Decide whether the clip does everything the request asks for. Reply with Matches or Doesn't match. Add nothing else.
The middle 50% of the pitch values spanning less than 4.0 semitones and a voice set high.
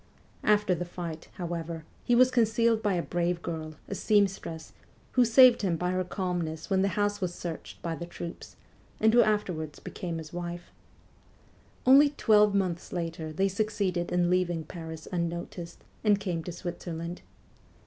Doesn't match